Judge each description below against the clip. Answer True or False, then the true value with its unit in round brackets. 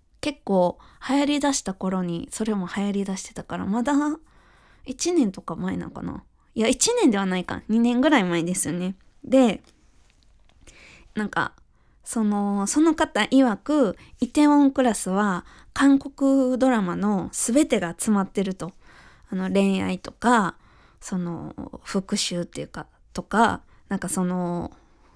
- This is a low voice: False (205 Hz)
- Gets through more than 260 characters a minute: False (255 characters per minute)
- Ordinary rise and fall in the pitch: False (6.1 semitones)